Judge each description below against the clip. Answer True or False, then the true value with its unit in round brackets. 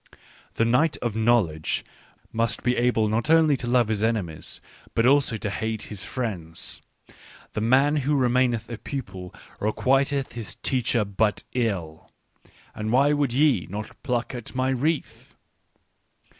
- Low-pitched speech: True (120 Hz)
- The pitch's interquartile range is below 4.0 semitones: True (3.6 semitones)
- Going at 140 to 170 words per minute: True (150 wpm)